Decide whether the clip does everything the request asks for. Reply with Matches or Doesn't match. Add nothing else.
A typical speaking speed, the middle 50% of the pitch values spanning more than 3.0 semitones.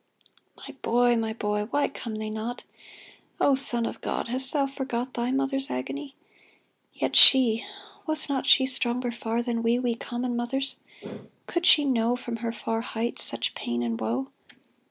Doesn't match